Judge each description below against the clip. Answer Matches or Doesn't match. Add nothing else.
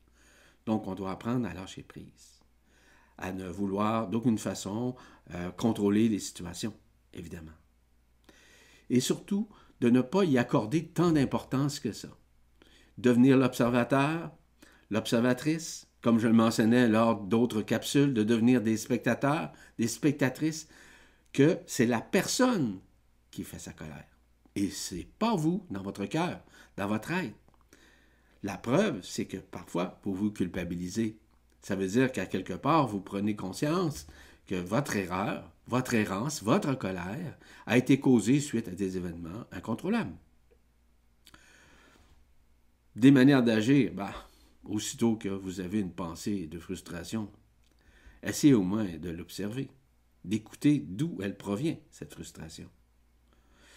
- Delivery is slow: Matches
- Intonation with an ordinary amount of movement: Doesn't match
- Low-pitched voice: Matches